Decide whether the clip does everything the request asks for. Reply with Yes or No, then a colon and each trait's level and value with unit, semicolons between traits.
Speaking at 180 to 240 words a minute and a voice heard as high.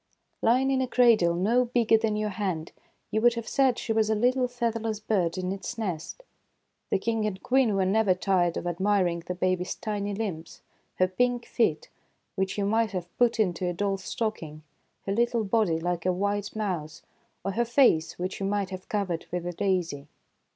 Yes: average, 190 wpm; high, 200 Hz